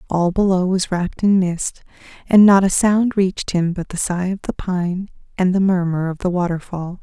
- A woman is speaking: Yes, female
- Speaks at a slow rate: No, fast, 205 wpm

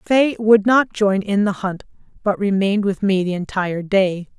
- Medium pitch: No, high, 200 Hz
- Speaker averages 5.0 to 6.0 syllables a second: No, 4.8 syllables/s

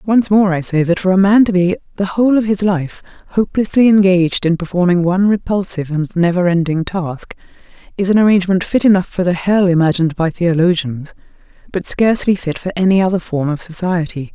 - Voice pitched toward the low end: No, medium, 185 Hz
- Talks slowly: No, average, 190 wpm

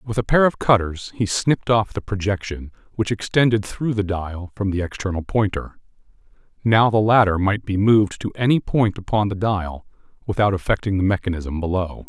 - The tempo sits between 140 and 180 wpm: Yes, average, 175 wpm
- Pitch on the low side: Yes, low, 100 Hz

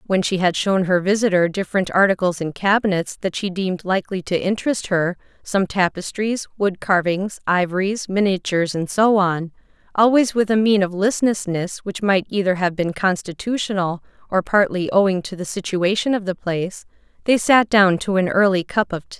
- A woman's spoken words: Yes, female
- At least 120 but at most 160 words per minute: No, average, 170 wpm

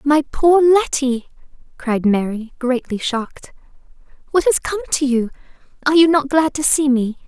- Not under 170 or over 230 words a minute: No, average, 155 wpm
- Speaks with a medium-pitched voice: No, very high, 270 Hz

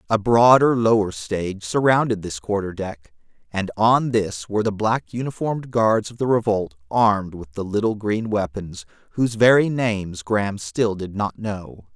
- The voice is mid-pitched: No, low, 105 Hz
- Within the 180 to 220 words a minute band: No, average, 165 wpm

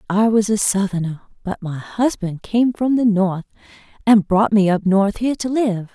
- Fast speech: No, average, 190 wpm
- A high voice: Yes, high, 205 Hz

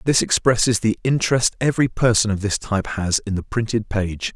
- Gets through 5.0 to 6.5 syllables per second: Yes, 5.6 syllables/s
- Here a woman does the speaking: No, male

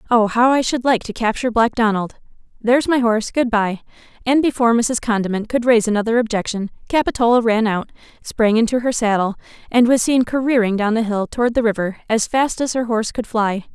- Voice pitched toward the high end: Yes, high, 230 Hz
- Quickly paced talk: No, average, 195 wpm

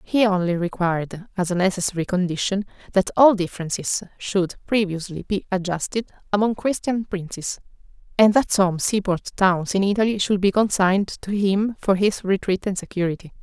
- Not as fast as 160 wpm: Yes, average, 150 wpm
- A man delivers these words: No, female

